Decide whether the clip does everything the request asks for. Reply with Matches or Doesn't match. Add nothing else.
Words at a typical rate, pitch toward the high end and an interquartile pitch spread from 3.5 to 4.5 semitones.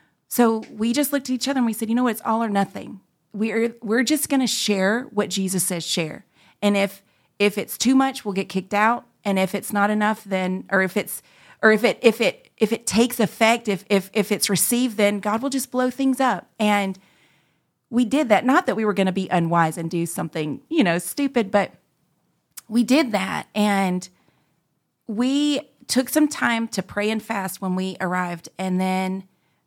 Doesn't match